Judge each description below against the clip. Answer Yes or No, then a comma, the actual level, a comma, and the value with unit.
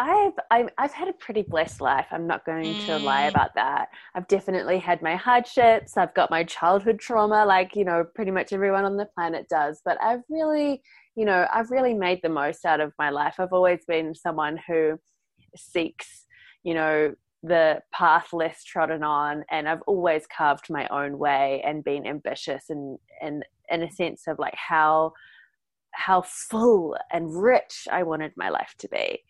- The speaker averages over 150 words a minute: Yes, average, 180 wpm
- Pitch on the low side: No, medium, 175 Hz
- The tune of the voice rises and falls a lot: Yes, wide, 5.8 semitones